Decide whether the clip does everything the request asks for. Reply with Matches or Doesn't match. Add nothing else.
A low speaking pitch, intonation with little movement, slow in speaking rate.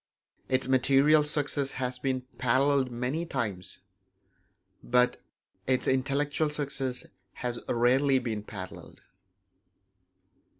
Matches